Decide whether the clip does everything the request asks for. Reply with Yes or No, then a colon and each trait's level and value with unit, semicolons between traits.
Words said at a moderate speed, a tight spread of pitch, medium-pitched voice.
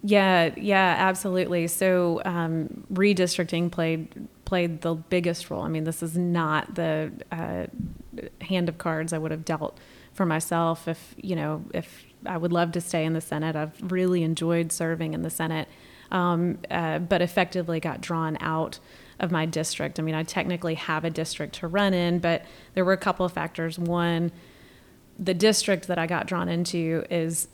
Yes: average, 180 wpm; narrow, 2.0 semitones; medium, 170 Hz